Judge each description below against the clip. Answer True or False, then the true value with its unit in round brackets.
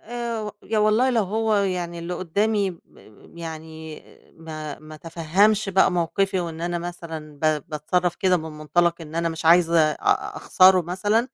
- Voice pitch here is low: False (175 Hz)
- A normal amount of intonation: True (3.6 semitones)